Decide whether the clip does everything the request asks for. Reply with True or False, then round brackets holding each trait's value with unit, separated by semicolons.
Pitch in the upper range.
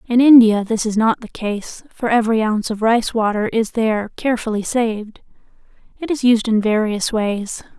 True (225 Hz)